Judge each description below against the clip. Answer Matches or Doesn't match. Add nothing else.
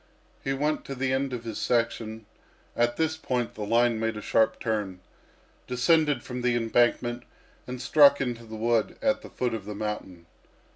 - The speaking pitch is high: Doesn't match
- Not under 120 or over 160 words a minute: Doesn't match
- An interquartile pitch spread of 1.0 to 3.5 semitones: Matches